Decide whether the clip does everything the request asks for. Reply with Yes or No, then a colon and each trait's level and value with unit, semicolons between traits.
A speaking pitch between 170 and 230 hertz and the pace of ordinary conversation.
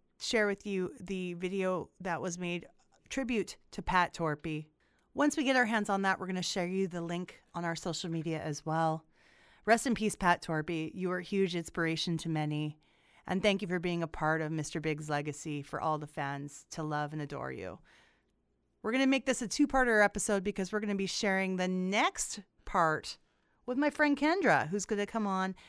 No: medium, 185 Hz; fast, 210 wpm